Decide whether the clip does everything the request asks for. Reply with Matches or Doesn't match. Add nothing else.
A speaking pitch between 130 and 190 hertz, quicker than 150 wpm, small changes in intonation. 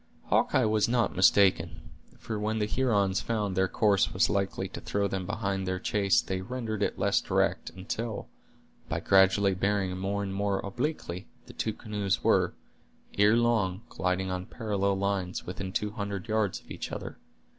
Doesn't match